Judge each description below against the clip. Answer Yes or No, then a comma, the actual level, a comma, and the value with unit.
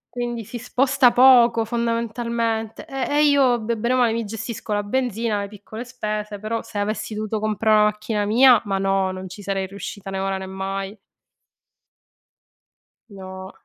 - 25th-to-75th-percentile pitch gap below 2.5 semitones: No, average, 2.8 semitones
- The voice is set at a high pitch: Yes, high, 220 Hz